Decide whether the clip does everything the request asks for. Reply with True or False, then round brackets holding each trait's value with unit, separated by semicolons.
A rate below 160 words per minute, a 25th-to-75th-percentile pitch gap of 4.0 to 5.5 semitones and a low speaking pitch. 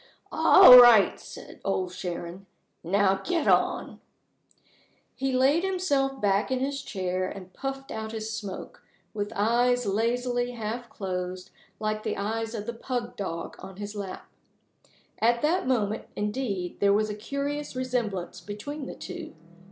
False (145 wpm; 4.4 semitones; 220 Hz)